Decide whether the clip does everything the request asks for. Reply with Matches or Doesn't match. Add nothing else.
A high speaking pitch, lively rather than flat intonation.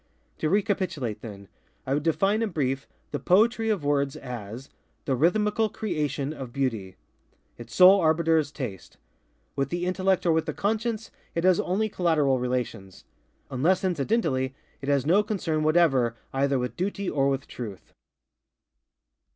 Doesn't match